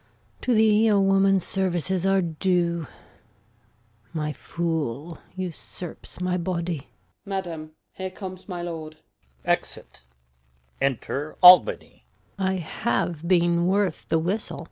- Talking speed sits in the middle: No, slow, 85 wpm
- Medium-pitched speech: Yes, medium, 180 Hz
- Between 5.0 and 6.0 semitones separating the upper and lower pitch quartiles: No, average, 2.8 semitones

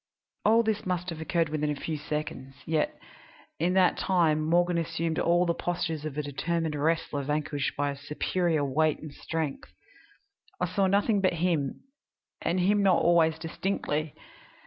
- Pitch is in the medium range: Yes, medium, 165 Hz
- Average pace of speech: Yes, average, 155 wpm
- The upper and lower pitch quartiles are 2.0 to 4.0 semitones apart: Yes, average, 2.8 semitones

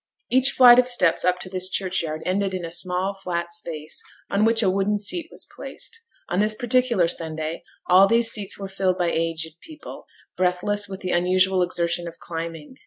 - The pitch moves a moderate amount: Yes, average, 3.2 semitones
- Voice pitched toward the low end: No, medium, 185 Hz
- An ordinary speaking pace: Yes, average, 185 wpm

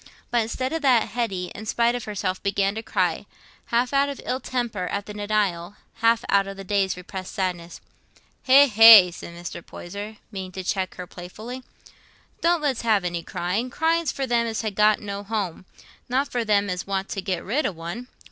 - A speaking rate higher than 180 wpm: Yes, average, 195 wpm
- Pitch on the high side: Yes, high, 205 Hz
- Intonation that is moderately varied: Yes, average, 4.3 semitones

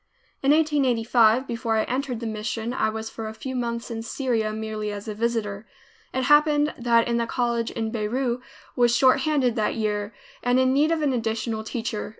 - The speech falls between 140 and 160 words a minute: No, average, 185 wpm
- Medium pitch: No, high, 235 Hz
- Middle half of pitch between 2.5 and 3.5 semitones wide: Yes, average, 2.8 semitones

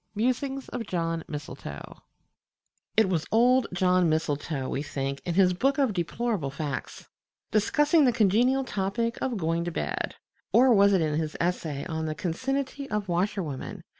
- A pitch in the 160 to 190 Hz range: Yes, medium, 185 Hz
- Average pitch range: No, wide, 7.1 semitones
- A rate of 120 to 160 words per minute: Yes, average, 155 wpm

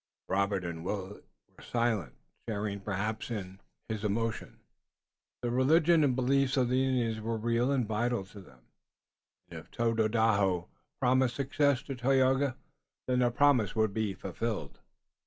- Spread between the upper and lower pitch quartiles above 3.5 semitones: Yes, average, 4.0 semitones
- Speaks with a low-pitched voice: Yes, low, 115 Hz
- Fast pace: No, average, 140 wpm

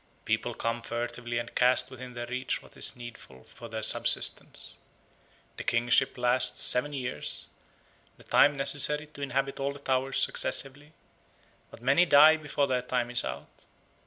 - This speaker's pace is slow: No, average, 155 wpm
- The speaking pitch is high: No, low, 130 Hz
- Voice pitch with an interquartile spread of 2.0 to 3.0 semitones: Yes, average, 2.7 semitones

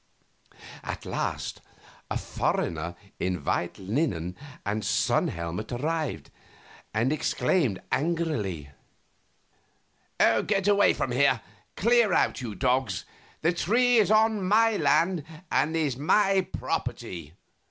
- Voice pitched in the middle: Yes, medium, 145 Hz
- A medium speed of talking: No, slow, 105 wpm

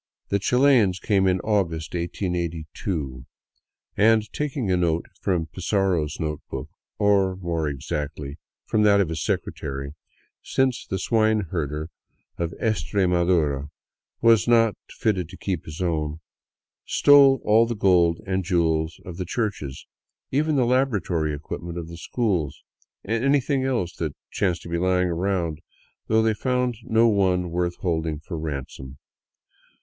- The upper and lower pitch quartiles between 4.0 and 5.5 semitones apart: Yes, average, 5.2 semitones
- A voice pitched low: Yes, very low, 90 Hz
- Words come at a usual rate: Yes, average, 145 wpm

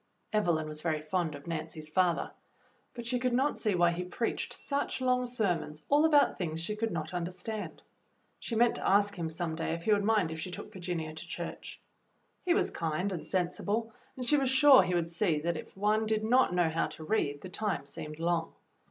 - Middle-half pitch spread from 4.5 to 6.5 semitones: Yes, average, 5.2 semitones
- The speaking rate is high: Yes, fast, 215 wpm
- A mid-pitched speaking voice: Yes, medium, 180 Hz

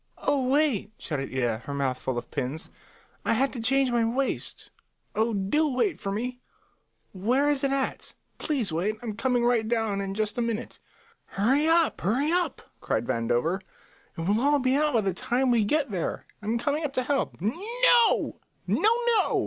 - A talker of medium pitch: No, high, 240 Hz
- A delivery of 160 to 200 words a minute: Yes, average, 180 wpm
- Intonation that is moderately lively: No, wide, 6.1 semitones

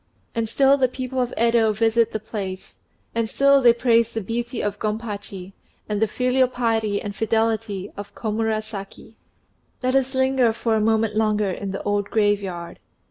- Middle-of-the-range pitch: No, high, 220 Hz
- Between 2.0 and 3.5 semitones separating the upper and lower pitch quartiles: Yes, narrow, 2.4 semitones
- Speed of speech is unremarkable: Yes, average, 165 wpm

